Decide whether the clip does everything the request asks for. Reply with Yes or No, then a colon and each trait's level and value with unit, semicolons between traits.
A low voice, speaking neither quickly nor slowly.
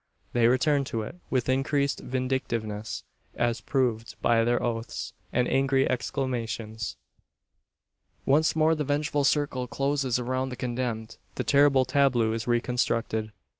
No: low, 125 Hz; slow, 130 wpm